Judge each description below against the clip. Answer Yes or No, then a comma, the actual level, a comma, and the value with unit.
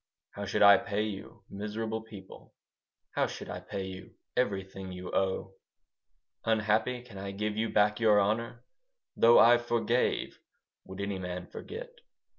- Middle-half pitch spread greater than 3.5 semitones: No, average, 2.8 semitones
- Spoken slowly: No, average, 145 wpm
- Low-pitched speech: Yes, low, 105 Hz